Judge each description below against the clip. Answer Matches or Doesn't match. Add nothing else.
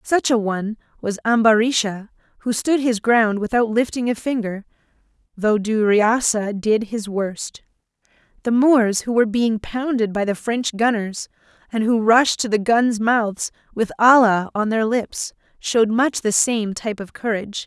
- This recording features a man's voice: Doesn't match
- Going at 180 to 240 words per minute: Doesn't match